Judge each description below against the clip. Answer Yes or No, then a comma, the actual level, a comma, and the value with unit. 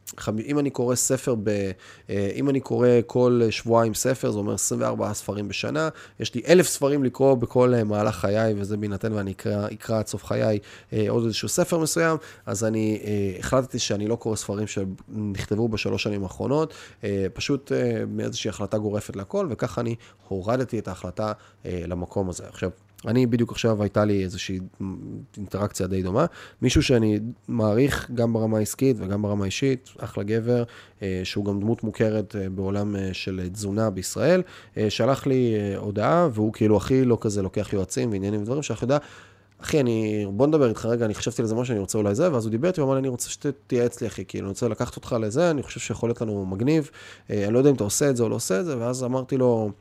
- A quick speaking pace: Yes, fast, 185 wpm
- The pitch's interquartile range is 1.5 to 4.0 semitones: Yes, average, 3.4 semitones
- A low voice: Yes, low, 110 Hz